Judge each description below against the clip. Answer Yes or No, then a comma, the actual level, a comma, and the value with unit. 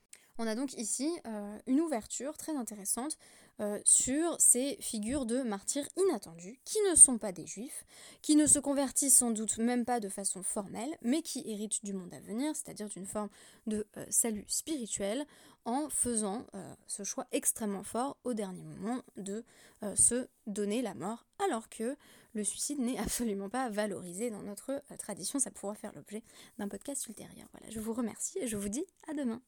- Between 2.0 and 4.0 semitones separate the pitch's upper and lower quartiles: No, average, 4.5 semitones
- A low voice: No, high, 230 Hz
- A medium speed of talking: Yes, average, 185 wpm